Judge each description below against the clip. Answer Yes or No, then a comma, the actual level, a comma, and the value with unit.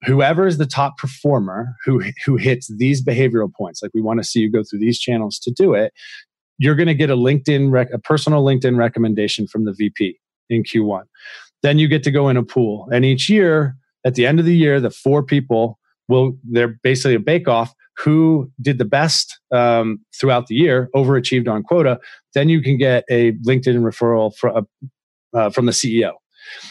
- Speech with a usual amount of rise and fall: Yes, average, 3.6 semitones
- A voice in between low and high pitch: No, low, 130 Hz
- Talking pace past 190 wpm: Yes, average, 200 wpm